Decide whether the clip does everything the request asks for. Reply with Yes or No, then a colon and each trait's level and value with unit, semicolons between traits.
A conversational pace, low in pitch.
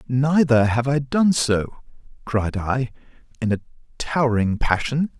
No: slow, 125 wpm; low, 125 Hz